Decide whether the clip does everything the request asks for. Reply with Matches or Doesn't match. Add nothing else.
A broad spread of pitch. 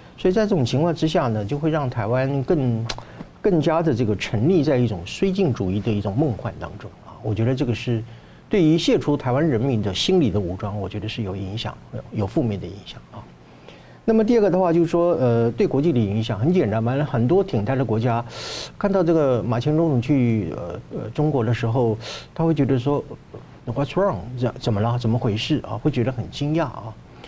Matches